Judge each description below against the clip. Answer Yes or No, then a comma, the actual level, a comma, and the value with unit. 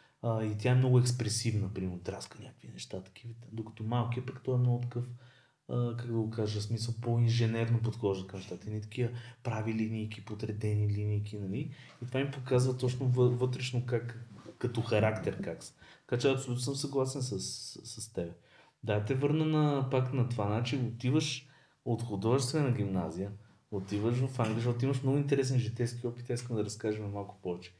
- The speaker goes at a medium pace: No, fast, 180 wpm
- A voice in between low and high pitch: No, low, 120 Hz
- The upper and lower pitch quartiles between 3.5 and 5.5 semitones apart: No, average, 3.1 semitones